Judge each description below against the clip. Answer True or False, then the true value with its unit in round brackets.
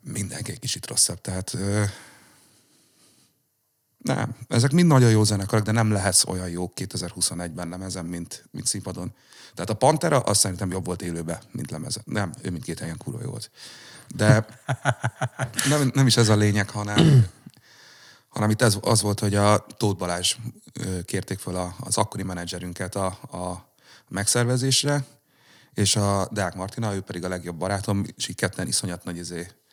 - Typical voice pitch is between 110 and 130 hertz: False (100 Hz)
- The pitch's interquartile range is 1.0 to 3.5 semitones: False (4.6 semitones)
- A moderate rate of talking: False (160 wpm)